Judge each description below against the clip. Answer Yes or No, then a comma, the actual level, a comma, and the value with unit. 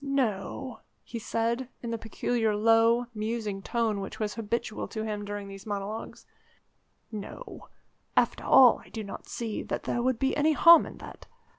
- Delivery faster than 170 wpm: No, average, 165 wpm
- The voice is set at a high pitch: Yes, high, 225 Hz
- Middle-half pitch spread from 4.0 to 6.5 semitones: No, narrow, 2.4 semitones